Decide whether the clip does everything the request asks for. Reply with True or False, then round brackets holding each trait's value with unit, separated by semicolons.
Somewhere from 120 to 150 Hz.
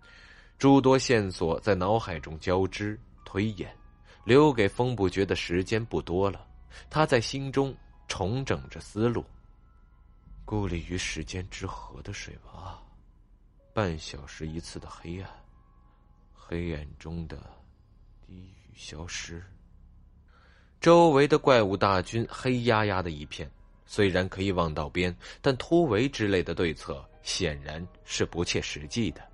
False (95 Hz)